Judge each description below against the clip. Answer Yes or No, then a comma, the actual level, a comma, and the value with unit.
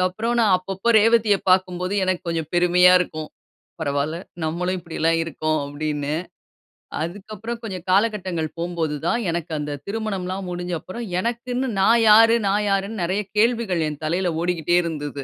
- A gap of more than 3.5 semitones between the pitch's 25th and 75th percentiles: Yes, average, 4.2 semitones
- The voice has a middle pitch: Yes, medium, 180 Hz